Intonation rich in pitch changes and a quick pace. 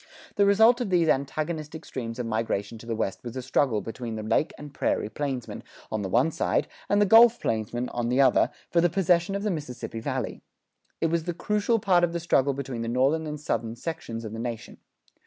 Yes: wide, 6.8 semitones; fast, 215 wpm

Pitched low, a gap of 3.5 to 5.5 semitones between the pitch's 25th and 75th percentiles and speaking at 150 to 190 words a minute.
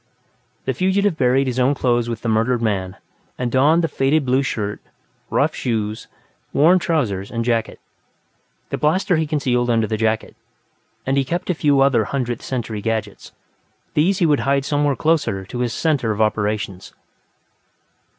Yes: low, 125 Hz; average, 4.7 semitones; average, 160 wpm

